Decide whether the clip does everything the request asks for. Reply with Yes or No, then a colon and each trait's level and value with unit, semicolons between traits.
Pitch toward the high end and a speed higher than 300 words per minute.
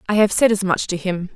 Yes: high, 195 Hz; fast, 310 wpm